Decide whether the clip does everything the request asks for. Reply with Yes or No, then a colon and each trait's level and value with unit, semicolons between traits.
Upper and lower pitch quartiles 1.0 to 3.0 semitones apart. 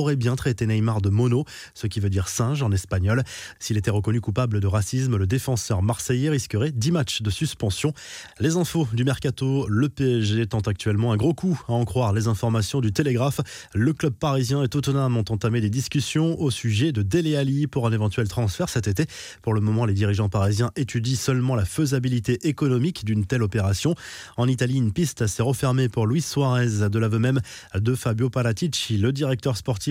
No: average, 4.1 semitones